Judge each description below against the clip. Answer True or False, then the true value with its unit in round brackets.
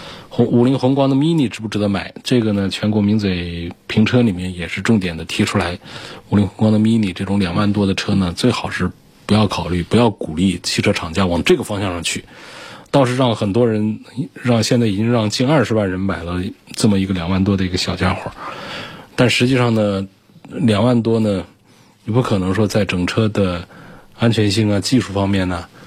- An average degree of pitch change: True (3.6 semitones)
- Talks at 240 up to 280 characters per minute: False (305 characters per minute)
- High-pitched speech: False (105 Hz)